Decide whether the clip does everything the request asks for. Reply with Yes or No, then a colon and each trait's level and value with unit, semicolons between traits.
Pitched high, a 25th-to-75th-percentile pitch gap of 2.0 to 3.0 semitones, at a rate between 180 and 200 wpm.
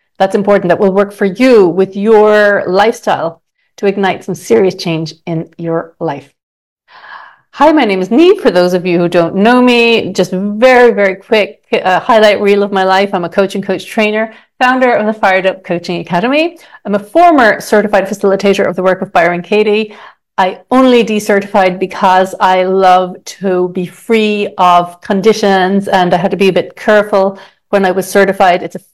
Yes: high, 195 Hz; narrow, 2.5 semitones; average, 185 wpm